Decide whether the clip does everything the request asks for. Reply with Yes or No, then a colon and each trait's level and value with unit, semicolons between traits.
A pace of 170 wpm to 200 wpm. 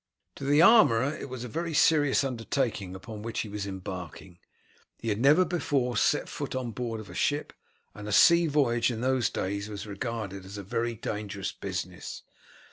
Yes: average, 185 wpm